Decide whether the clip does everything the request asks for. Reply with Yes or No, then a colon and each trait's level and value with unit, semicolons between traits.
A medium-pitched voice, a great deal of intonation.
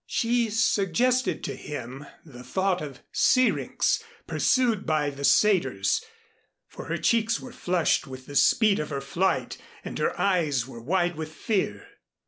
Yes: medium, 180 Hz; wide, 7.6 semitones